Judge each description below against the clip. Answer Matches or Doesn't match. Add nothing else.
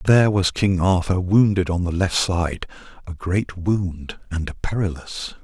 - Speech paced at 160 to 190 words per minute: Matches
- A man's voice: Matches